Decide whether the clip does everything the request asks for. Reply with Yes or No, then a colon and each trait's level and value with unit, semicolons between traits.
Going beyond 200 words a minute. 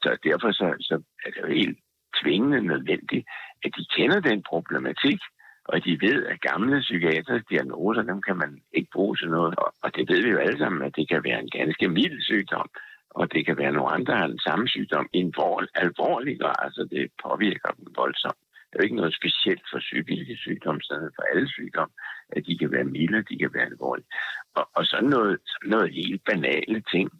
Yes: average, 210 wpm